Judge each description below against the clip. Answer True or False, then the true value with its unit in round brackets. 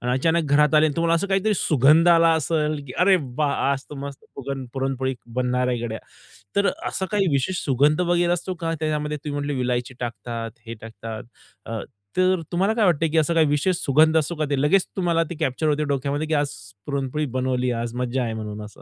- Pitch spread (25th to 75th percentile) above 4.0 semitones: True (4.6 semitones)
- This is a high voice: False (145 Hz)